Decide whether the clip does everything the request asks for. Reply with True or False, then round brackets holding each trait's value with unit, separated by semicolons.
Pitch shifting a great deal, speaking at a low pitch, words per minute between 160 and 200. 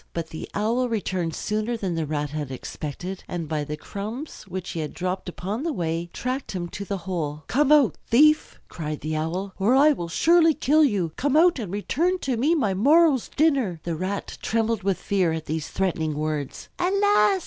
False (8.1 semitones; 195 Hz; 195 wpm)